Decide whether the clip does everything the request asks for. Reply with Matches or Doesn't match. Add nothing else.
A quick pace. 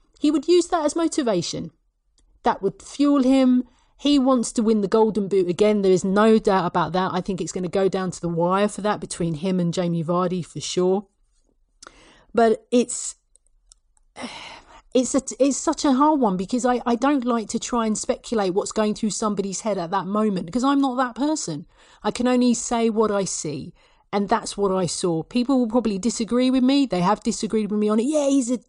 Matches